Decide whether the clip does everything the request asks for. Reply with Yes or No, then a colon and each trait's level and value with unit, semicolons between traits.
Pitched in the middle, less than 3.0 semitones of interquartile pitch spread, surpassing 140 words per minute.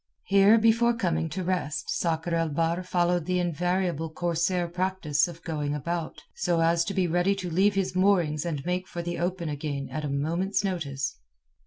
Yes: medium, 175 Hz; narrow, 2.4 semitones; average, 180 wpm